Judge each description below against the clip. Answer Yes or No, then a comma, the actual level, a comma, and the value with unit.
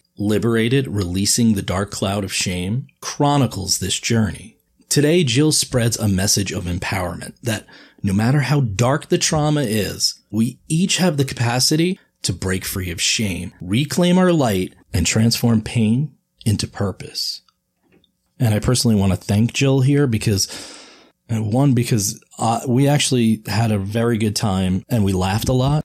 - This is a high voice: No, low, 115 Hz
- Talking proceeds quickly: No, average, 160 wpm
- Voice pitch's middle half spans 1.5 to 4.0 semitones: No, average, 5.2 semitones